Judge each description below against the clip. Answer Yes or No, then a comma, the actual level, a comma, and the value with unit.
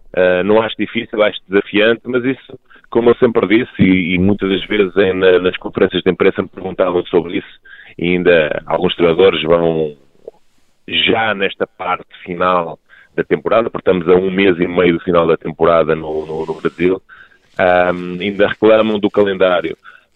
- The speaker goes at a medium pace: Yes, average, 175 wpm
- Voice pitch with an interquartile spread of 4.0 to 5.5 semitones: No, average, 2.7 semitones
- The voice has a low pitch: Yes, very low, 90 Hz